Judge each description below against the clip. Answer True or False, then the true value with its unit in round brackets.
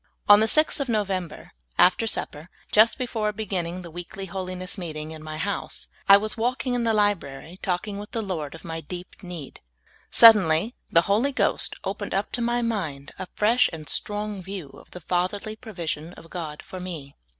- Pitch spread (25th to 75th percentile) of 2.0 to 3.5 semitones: False (4.5 semitones)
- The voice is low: False (190 Hz)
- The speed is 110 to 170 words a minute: False (185 wpm)